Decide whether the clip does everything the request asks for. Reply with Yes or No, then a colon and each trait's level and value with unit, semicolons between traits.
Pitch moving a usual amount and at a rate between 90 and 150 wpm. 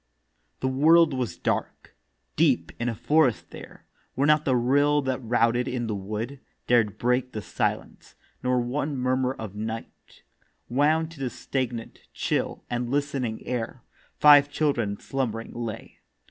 Yes: average, 3.3 semitones; average, 145 wpm